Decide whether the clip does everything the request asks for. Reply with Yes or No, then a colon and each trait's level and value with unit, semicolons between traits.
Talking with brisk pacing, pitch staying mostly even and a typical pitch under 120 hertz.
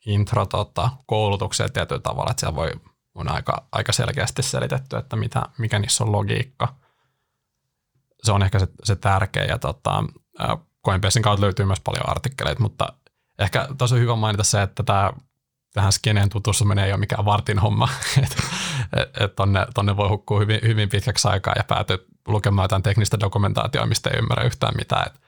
No: fast, 165 wpm; average, 3.4 semitones; low, 110 Hz